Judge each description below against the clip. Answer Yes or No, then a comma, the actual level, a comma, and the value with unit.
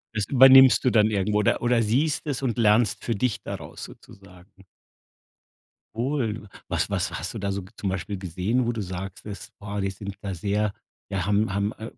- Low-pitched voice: Yes, low, 105 Hz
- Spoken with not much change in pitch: No, average, 3.1 semitones